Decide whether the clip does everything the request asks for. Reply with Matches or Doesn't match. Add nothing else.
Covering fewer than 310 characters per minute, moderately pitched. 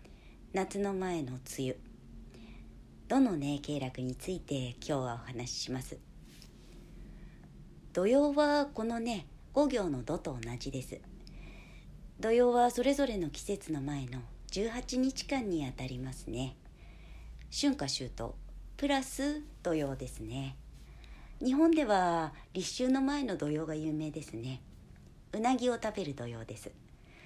Matches